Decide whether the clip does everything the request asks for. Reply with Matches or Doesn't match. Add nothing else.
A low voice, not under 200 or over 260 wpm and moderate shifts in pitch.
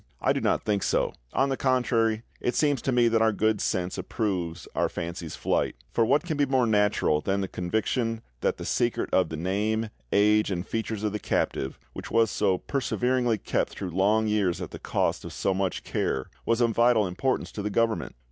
Matches